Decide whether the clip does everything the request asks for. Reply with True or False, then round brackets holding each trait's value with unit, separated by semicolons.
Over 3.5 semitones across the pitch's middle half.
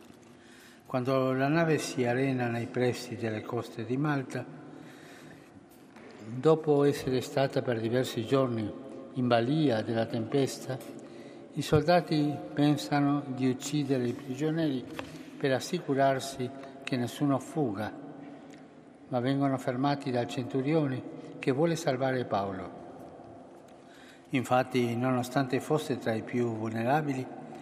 False (2.9 semitones)